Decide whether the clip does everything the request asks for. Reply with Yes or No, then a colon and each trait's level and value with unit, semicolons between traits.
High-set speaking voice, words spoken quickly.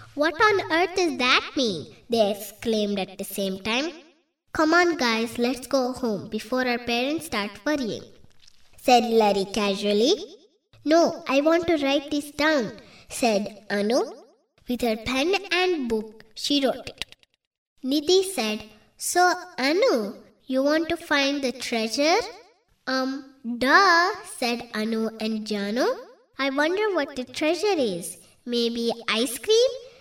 Yes: very high, 265 Hz; fast, 135 wpm